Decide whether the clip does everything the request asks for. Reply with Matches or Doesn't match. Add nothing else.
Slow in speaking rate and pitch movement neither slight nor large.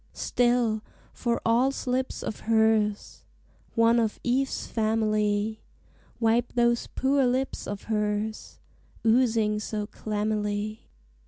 Doesn't match